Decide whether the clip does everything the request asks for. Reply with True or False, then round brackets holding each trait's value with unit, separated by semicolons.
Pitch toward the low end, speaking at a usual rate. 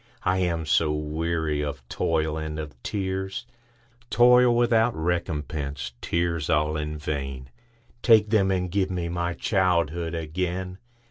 False (85 Hz; 120 wpm)